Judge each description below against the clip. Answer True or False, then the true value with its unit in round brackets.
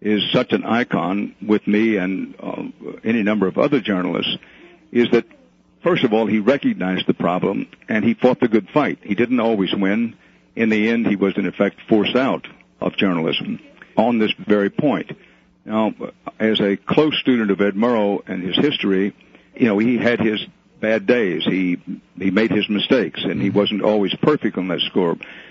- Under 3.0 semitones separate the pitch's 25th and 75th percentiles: True (2.6 semitones)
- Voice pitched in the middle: False (105 Hz)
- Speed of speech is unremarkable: True (185 wpm)